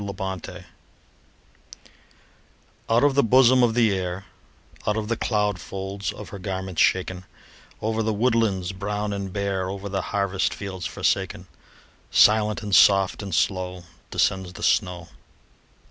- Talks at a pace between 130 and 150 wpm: Yes, average, 140 wpm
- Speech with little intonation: Yes, narrow, 2.3 semitones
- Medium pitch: No, low, 100 Hz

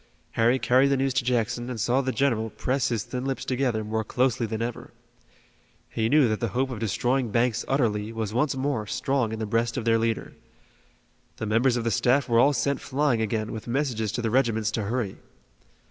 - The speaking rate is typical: No, fast, 210 wpm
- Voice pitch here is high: No, low, 120 Hz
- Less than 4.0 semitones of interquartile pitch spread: Yes, average, 2.8 semitones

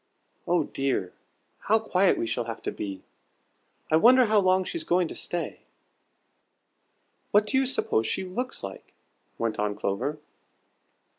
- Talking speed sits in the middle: Yes, average, 145 wpm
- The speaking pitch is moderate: Yes, medium, 175 Hz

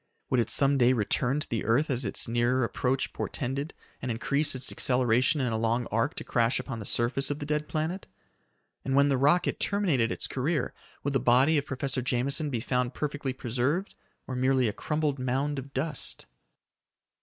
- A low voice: Yes, low, 130 Hz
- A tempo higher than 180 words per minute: Yes, average, 190 wpm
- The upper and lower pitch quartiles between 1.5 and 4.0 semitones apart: Yes, average, 2.8 semitones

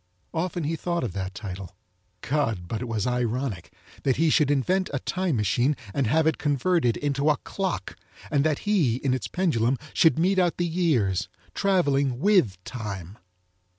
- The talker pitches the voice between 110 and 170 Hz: Yes, medium, 140 Hz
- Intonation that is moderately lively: No, wide, 6.5 semitones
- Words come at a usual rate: Yes, average, 170 wpm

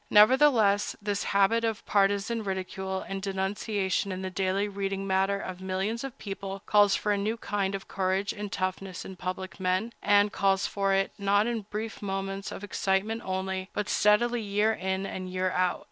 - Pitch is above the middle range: Yes, high, 195 Hz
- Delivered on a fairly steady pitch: Yes, narrow, 1.5 semitones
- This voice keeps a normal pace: Yes, average, 175 wpm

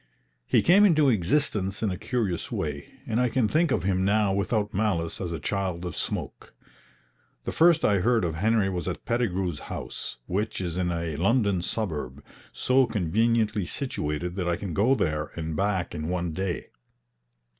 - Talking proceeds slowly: No, average, 175 wpm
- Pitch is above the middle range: No, very low, 95 Hz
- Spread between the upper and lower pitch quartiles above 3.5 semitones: Yes, average, 4.6 semitones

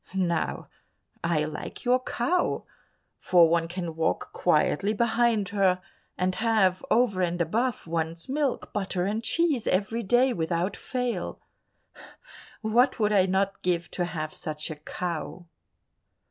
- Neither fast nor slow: No, slow, 130 wpm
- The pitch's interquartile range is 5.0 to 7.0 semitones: Yes, average, 5.3 semitones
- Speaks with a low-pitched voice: No, high, 190 Hz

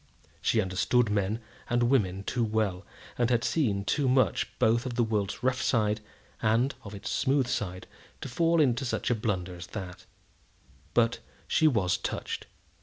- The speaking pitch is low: Yes, low, 110 Hz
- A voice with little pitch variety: No, average, 3.9 semitones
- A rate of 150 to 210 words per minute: Yes, average, 165 wpm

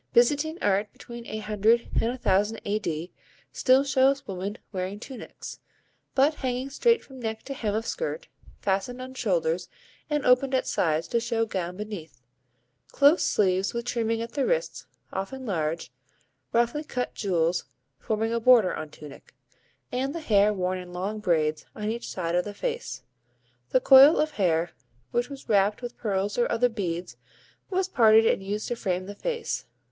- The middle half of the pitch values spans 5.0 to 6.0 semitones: Yes, average, 5.3 semitones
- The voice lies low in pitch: No, high, 225 Hz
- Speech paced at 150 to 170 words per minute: Yes, average, 165 wpm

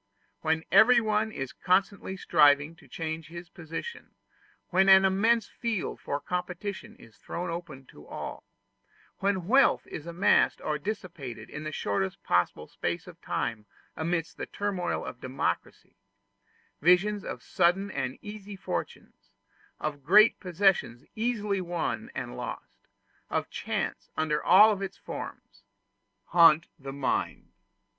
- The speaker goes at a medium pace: No, slow, 130 wpm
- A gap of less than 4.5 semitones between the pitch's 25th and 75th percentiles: No, average, 5.2 semitones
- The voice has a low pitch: No, medium, 175 Hz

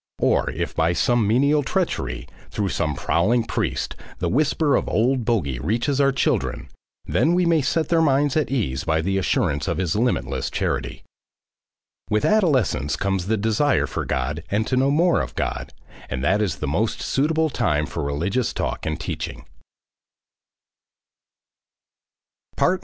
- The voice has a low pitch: Yes, low, 110 Hz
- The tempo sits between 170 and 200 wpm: No, average, 150 wpm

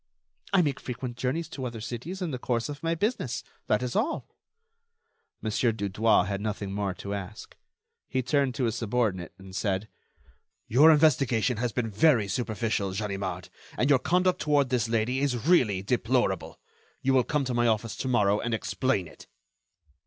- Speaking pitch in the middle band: No, low, 120 Hz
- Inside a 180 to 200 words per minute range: No, average, 170 wpm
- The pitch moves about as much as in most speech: Yes, average, 4.6 semitones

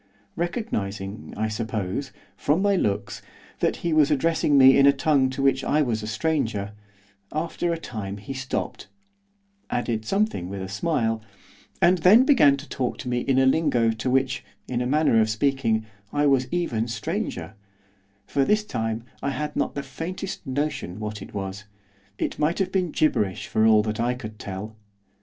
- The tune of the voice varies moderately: No, wide, 6.0 semitones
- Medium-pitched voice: No, low, 130 Hz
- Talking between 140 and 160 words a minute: No, average, 175 wpm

